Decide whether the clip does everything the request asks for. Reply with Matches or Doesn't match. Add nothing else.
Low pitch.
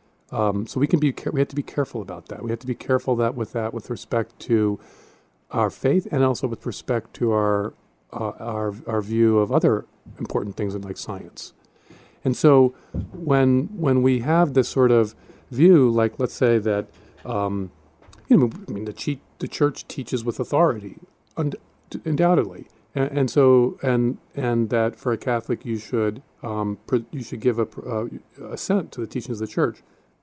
Matches